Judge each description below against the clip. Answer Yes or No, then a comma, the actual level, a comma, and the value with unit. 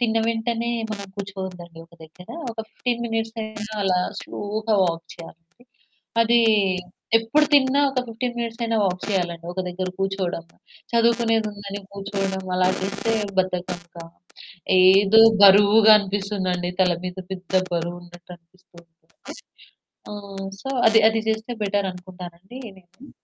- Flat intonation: No, average, 3.6 semitones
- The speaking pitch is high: Yes, high, 195 Hz